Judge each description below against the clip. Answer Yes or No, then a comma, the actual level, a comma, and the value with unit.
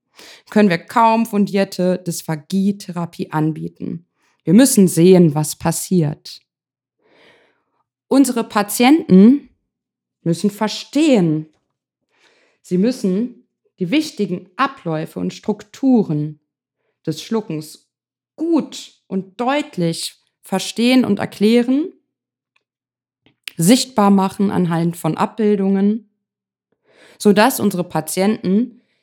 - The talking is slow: Yes, slow, 80 wpm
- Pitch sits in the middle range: No, high, 205 Hz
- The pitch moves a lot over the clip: Yes, wide, 6.1 semitones